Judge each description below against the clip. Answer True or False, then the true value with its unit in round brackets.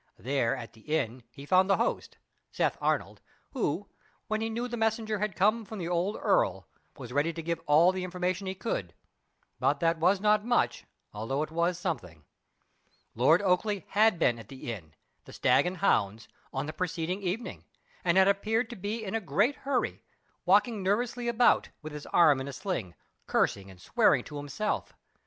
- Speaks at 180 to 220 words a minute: True (185 wpm)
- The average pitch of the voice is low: False (180 Hz)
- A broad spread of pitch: True (6.8 semitones)